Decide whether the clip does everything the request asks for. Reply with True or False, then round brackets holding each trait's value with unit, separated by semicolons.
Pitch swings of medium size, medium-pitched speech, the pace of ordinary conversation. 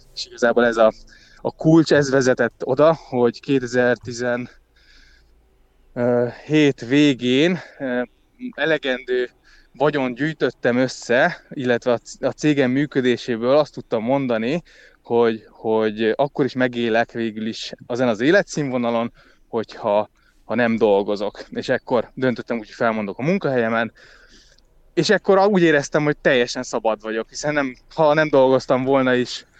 False (3.5 semitones; 125 Hz; 120 wpm)